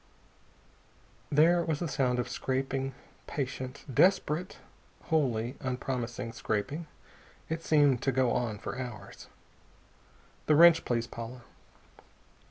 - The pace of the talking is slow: Yes, slow, 105 wpm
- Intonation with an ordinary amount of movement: Yes, average, 3.8 semitones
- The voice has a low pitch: Yes, low, 130 Hz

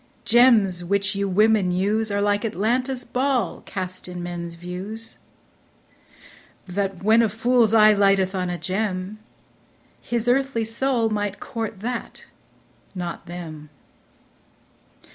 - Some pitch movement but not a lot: Yes, average, 3.6 semitones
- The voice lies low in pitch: No, high, 205 Hz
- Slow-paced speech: Yes, slow, 120 wpm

